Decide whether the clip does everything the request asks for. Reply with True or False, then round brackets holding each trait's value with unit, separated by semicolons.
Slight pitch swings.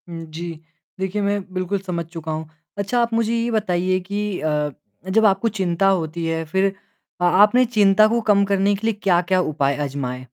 False (3.7 semitones)